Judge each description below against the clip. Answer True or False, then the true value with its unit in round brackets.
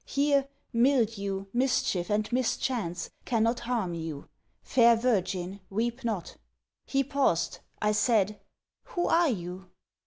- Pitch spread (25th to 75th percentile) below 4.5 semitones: False (4.8 semitones)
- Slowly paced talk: True (115 wpm)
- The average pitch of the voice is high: True (225 Hz)